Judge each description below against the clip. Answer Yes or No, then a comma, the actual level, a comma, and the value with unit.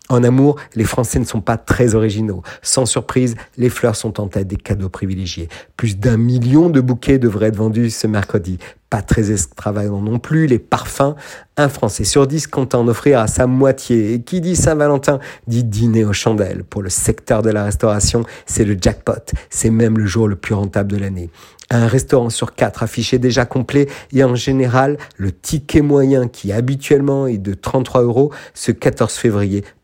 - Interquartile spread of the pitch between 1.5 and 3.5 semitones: No, average, 3.9 semitones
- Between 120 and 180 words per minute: No, average, 190 wpm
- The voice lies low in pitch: Yes, low, 120 Hz